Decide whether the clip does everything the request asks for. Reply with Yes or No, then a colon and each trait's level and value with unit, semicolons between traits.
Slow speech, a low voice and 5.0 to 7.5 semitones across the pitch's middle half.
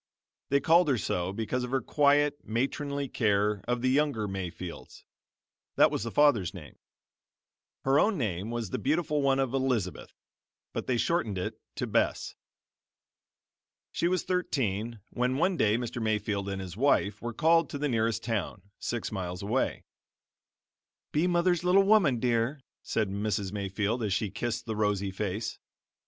No: average, 155 wpm; low, 115 Hz; wide, 5.6 semitones